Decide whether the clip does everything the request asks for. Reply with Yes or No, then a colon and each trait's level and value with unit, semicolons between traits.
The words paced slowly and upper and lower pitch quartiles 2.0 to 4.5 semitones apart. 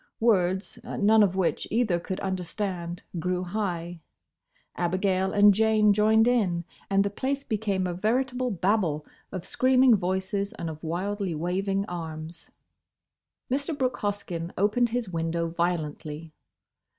Yes: slow, 125 wpm; average, 3.8 semitones